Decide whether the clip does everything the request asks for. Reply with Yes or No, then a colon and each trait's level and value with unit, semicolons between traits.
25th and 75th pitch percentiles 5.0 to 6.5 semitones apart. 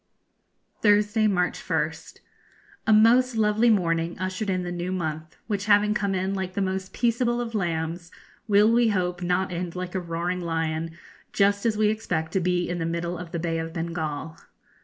No: average, 3.6 semitones